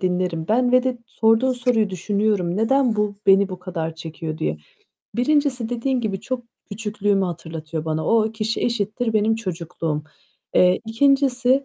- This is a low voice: No, high, 215 Hz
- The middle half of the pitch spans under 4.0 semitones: No, average, 5.3 semitones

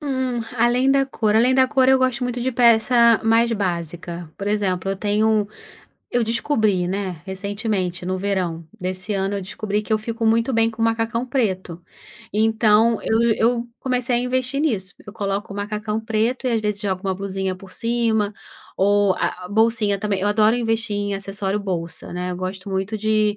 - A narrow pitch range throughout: No, average, 3.1 semitones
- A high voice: Yes, high, 215 Hz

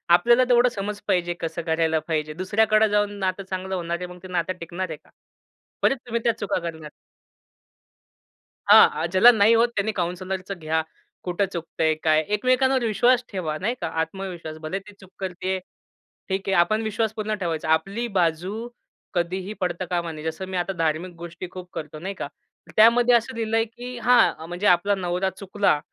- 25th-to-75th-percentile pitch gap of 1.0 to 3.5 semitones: No, average, 4.0 semitones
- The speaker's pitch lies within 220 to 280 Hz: No, medium, 185 Hz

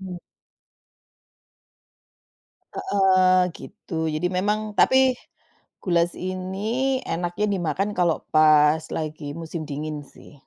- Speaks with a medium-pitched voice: Yes, medium, 180 Hz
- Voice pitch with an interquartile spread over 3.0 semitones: Yes, average, 4.2 semitones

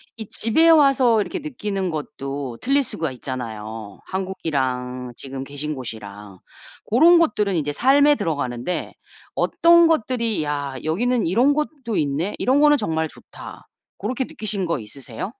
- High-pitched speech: No, medium, 180 Hz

